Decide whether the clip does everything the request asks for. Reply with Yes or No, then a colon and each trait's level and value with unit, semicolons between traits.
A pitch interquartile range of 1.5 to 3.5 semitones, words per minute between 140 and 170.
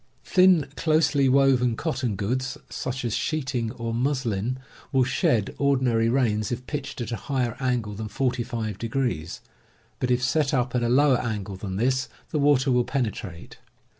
Yes: average, 3.1 semitones; average, 155 wpm